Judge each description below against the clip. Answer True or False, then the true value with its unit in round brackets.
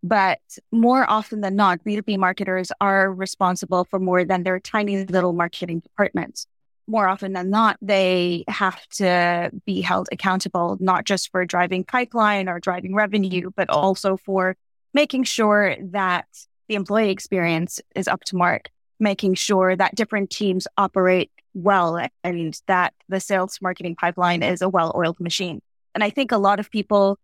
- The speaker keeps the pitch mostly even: True (2.1 semitones)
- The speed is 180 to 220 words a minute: False (160 wpm)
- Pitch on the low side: False (190 Hz)